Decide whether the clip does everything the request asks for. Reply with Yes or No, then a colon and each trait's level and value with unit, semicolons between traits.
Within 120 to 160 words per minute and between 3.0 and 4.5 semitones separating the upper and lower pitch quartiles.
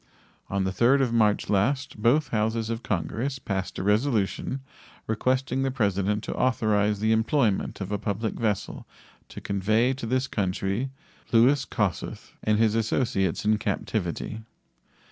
Yes: average, 145 wpm; average, 3.7 semitones